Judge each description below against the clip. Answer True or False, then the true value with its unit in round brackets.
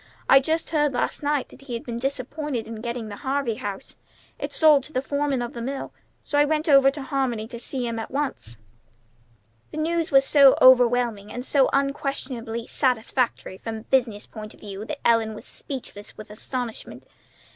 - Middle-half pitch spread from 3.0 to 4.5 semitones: True (3.5 semitones)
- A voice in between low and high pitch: False (255 Hz)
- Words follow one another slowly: False (190 wpm)